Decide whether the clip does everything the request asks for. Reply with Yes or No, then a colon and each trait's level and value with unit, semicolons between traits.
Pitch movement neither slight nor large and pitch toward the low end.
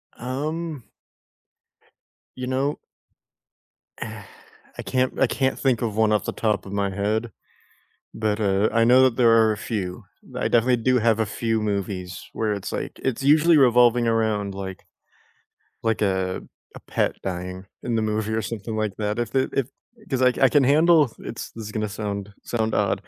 Yes: average, 3.5 semitones; low, 110 Hz